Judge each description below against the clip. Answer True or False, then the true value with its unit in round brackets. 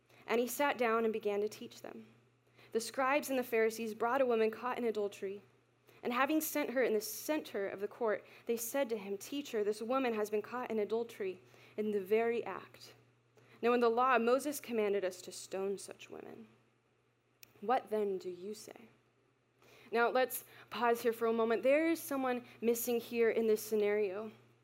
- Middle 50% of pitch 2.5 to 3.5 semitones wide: True (3.1 semitones)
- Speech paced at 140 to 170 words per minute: False (190 wpm)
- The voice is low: False (225 Hz)